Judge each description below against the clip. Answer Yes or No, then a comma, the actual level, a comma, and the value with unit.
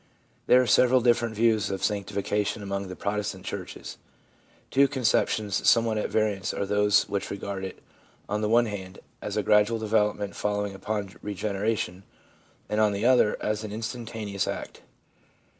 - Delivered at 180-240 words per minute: No, average, 155 wpm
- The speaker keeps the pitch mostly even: Yes, narrow, 1.9 semitones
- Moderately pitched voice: No, low, 105 Hz